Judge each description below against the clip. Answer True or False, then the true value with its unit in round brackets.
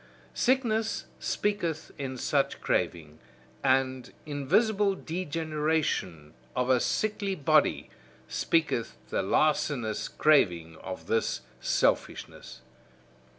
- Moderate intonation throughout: False (7.8 semitones)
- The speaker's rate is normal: False (85 wpm)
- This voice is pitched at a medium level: True (145 Hz)